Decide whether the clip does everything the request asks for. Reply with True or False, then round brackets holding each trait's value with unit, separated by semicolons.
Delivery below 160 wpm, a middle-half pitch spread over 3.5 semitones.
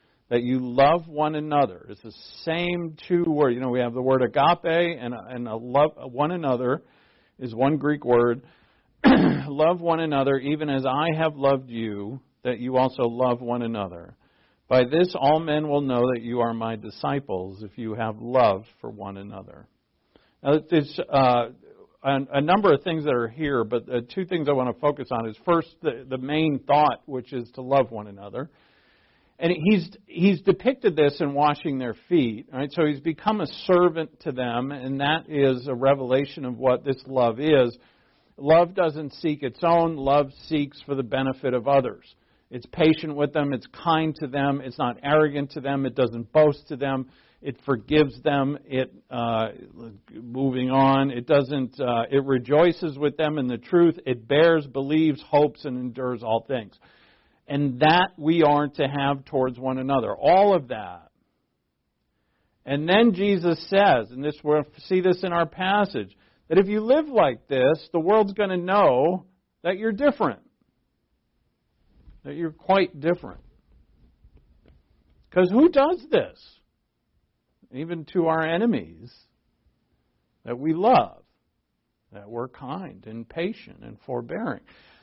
False (165 wpm; 4.5 semitones)